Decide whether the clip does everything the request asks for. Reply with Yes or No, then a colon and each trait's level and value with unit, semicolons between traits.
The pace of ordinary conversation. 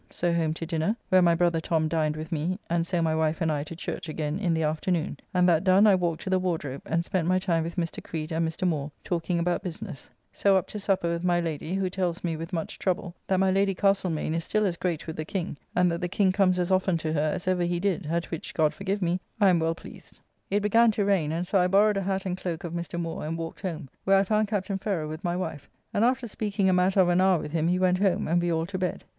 No: fast, 280 wpm